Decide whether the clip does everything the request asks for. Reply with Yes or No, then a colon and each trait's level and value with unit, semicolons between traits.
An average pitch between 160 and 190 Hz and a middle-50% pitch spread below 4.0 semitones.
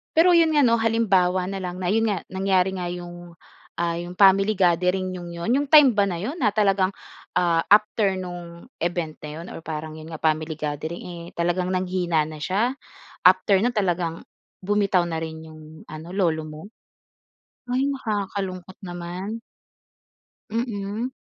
Yes: medium, 185 Hz; average, 3.2 semitones